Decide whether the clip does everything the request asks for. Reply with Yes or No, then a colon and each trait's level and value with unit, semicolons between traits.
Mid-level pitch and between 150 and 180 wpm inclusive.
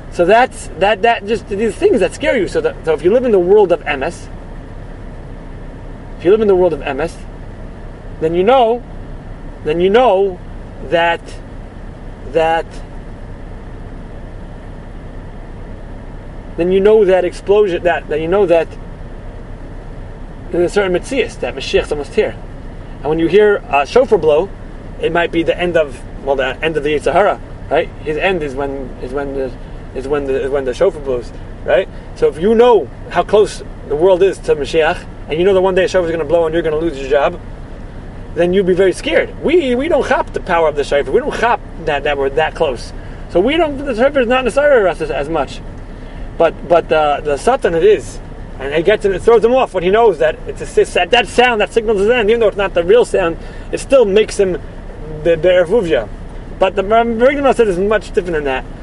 No: medium, 170 Hz; fast, 205 wpm